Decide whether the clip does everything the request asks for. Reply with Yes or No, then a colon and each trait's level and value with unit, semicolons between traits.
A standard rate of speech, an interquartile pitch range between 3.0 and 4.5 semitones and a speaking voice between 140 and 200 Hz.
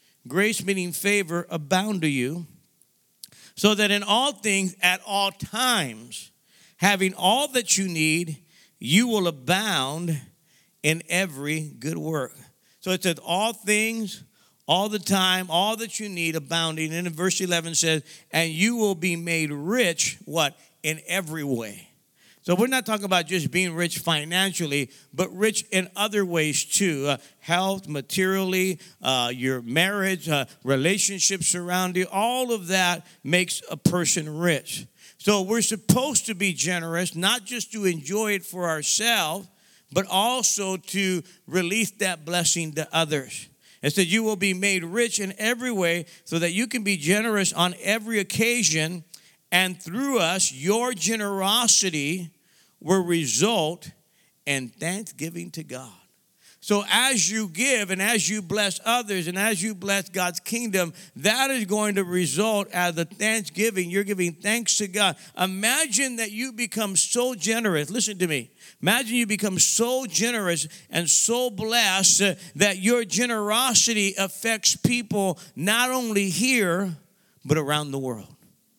Yes: average, 150 wpm; average, 4.1 semitones; medium, 185 Hz